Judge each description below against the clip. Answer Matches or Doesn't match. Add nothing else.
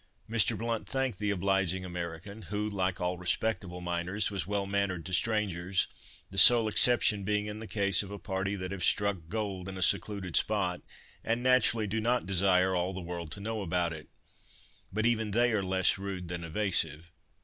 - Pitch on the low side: Matches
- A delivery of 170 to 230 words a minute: Matches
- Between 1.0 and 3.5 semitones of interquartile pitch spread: Matches